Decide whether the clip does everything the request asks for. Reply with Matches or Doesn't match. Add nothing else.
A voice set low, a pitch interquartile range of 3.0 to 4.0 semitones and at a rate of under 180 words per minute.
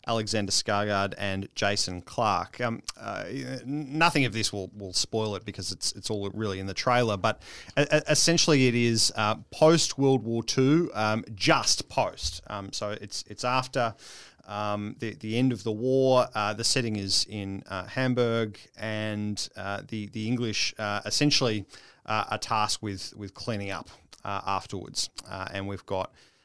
Matches